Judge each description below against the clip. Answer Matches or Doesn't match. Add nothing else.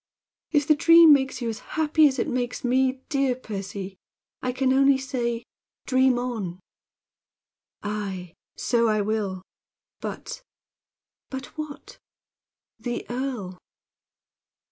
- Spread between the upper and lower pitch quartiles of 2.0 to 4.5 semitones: Matches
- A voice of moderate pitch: Doesn't match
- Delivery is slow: Matches